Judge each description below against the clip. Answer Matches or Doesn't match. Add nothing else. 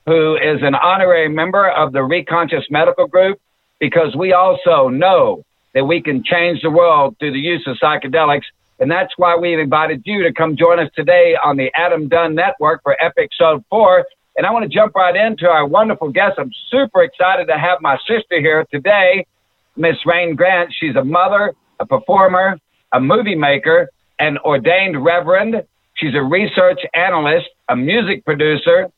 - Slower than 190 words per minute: Matches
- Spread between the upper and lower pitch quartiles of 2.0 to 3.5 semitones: Doesn't match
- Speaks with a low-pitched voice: Doesn't match